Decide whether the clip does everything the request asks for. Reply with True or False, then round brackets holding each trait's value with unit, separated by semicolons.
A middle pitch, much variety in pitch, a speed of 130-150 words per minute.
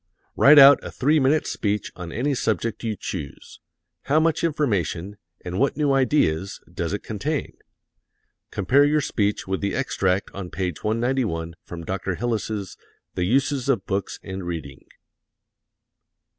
False (105 Hz; 6.8 semitones; 145 wpm)